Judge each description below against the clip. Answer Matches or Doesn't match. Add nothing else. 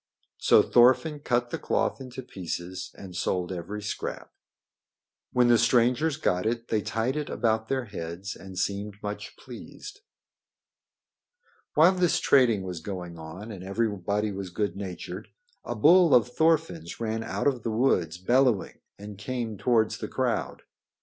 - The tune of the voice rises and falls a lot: Doesn't match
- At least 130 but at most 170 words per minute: Matches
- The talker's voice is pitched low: Matches